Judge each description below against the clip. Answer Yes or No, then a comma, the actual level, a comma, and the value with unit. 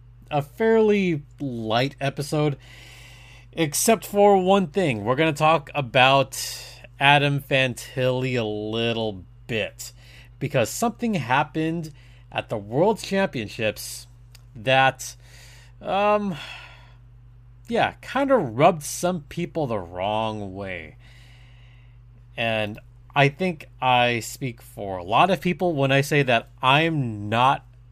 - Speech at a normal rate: No, slow, 110 wpm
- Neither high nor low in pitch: No, low, 125 Hz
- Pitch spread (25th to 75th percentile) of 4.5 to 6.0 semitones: No, average, 3.8 semitones